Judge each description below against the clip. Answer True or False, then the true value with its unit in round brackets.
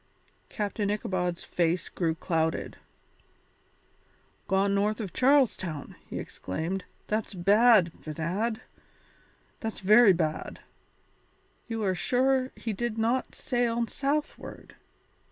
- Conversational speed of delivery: False (100 wpm)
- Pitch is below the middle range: False (205 Hz)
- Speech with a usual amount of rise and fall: True (4.9 semitones)